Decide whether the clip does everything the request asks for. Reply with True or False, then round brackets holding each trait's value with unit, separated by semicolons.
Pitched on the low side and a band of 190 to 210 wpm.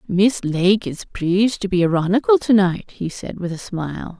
False (190 Hz; 200 wpm)